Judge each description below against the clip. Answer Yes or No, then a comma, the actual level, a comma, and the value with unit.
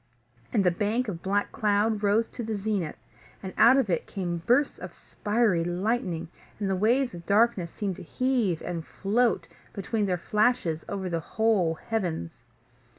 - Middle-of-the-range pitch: No, high, 205 Hz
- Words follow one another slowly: No, average, 160 wpm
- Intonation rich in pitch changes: No, average, 4.2 semitones